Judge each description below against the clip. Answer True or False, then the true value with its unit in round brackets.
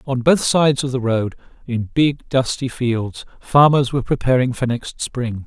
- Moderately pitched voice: False (125 Hz)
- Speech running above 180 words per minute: False (175 wpm)